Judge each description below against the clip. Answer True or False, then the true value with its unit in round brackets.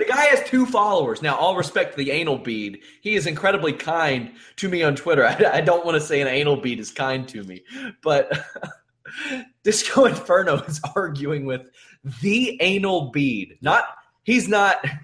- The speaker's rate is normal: True (180 wpm)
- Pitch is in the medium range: True (170 Hz)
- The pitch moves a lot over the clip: True (7.3 semitones)